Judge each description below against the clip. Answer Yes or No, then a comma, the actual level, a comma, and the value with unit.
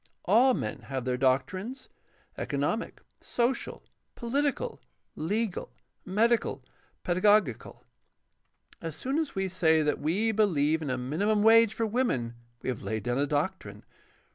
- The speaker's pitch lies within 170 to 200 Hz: Yes, high, 190 Hz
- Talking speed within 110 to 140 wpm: Yes, slow, 135 wpm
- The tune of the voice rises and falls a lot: Yes, wide, 8.0 semitones